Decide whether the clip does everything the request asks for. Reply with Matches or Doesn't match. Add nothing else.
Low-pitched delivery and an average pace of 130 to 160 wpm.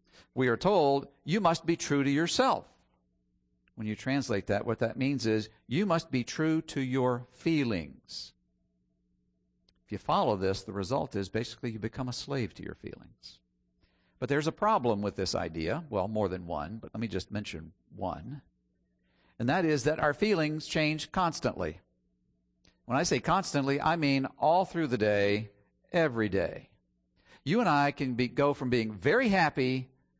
Doesn't match